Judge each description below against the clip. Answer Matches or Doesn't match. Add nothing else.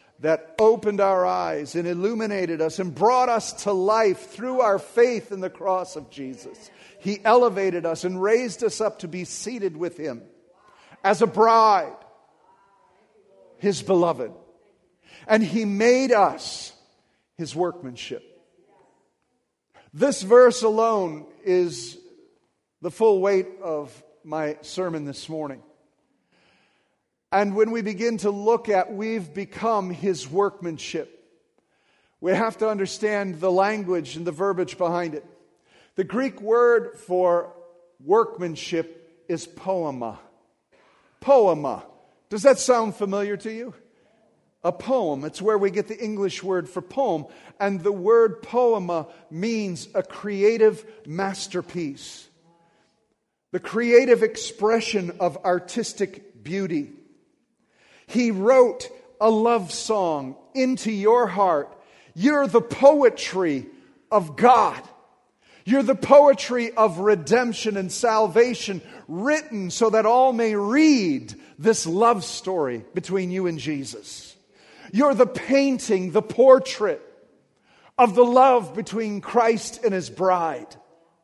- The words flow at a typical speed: Doesn't match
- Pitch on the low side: Doesn't match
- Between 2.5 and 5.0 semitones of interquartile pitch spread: Matches